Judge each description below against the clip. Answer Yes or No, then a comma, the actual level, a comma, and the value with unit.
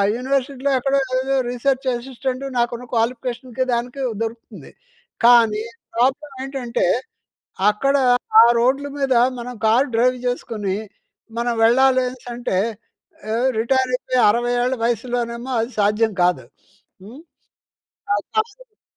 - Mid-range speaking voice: No, high, 245 Hz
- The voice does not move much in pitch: Yes, narrow, 2.2 semitones